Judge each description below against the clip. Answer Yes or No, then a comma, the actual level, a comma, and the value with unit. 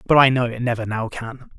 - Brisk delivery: Yes, fast, 265 wpm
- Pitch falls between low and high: No, low, 120 Hz